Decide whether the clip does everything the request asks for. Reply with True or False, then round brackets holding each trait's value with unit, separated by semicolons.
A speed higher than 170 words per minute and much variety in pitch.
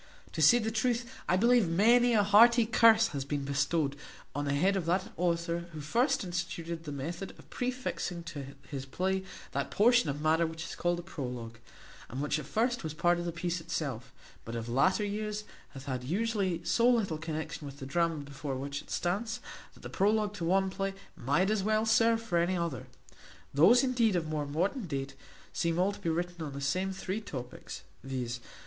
True (200 wpm; 6.4 semitones)